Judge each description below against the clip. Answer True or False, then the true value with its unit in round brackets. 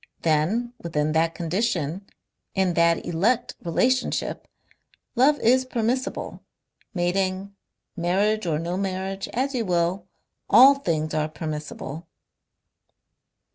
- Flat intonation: False (5.6 semitones)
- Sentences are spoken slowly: True (100 wpm)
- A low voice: False (185 Hz)